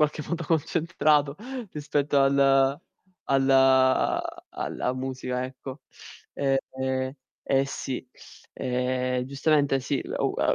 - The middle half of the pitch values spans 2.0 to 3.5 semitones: No, narrow, 1.5 semitones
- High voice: No, low, 135 Hz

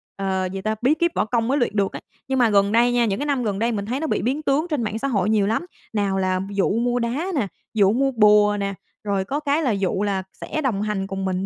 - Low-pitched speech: No, high, 215 Hz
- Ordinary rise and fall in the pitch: Yes, average, 4.4 semitones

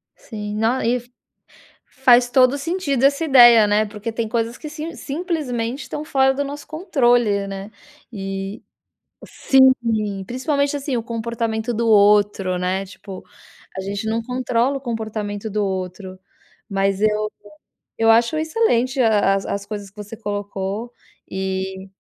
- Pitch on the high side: Yes, high, 225 Hz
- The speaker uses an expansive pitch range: No, average, 4.4 semitones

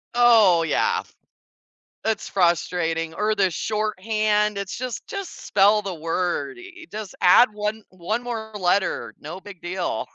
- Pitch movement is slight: No, average, 3.7 semitones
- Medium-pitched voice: No, high, 205 Hz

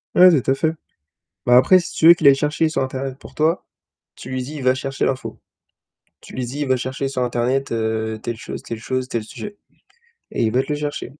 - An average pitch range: Yes, average, 3.2 semitones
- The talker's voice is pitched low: Yes, low, 130 Hz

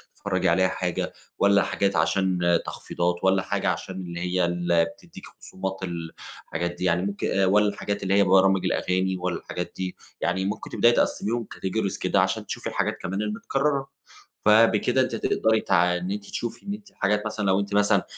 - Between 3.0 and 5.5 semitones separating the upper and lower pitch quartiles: No, narrow, 2.6 semitones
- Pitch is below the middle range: Yes, very low, 95 Hz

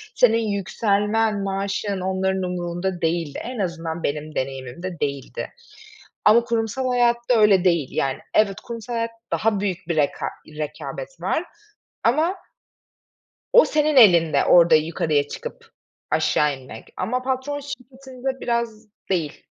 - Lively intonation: Yes, wide, 6.1 semitones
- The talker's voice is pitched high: Yes, high, 200 Hz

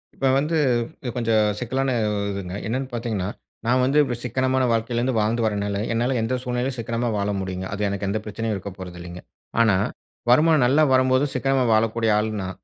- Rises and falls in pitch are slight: No, average, 3.9 semitones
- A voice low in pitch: Yes, low, 115 Hz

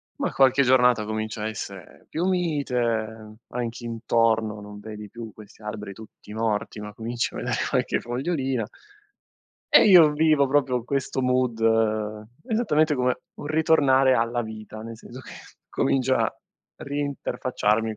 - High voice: No, low, 120 Hz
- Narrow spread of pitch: No, average, 3.8 semitones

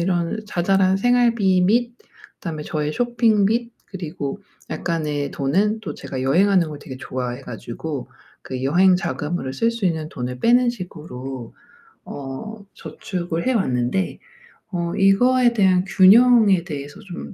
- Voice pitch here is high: No, medium, 180 Hz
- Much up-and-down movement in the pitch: Yes, wide, 6.4 semitones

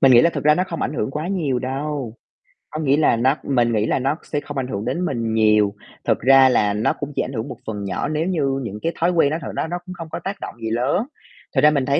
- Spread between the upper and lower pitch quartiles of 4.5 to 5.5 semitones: Yes, average, 4.9 semitones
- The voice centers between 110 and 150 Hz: Yes, low, 135 Hz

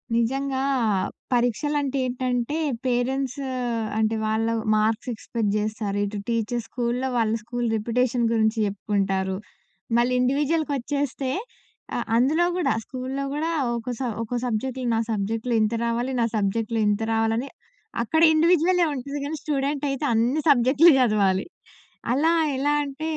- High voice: Yes, high, 245 Hz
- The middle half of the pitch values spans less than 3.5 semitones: No, average, 3.8 semitones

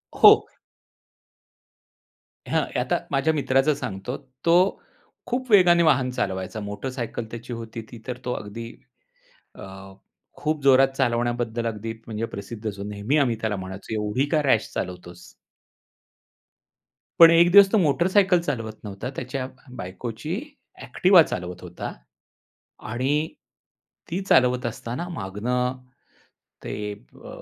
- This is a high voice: No, low, 120 Hz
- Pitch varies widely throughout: Yes, wide, 6.1 semitones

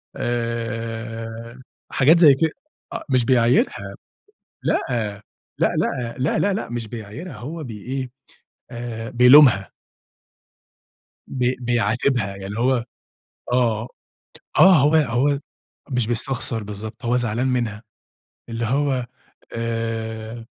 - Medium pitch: No, low, 120 Hz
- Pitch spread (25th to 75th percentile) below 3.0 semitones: Yes, narrow, 2.4 semitones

